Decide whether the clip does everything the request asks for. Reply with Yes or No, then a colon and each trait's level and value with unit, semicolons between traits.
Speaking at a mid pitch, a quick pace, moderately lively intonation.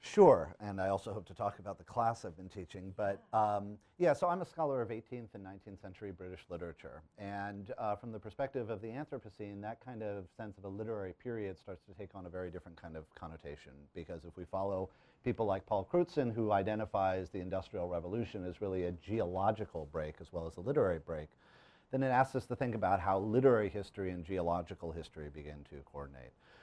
No: low, 100 Hz; fast, 210 wpm; average, 3.7 semitones